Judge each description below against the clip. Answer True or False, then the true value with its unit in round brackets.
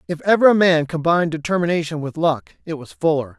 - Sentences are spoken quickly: False (195 wpm)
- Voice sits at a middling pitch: True (165 Hz)